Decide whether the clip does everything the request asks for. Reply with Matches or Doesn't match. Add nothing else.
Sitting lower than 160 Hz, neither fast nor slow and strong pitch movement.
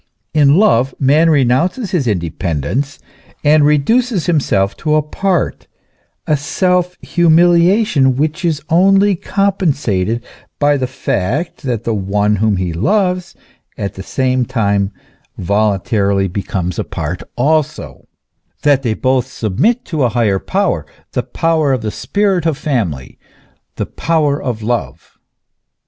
Doesn't match